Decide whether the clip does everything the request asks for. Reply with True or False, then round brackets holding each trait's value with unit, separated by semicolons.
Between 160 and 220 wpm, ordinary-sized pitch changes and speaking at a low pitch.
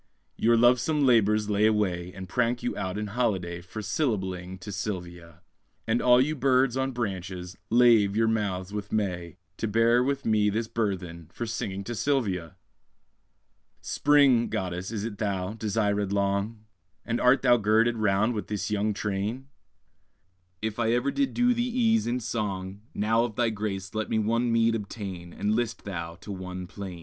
True (170 wpm; 3.6 semitones; 105 Hz)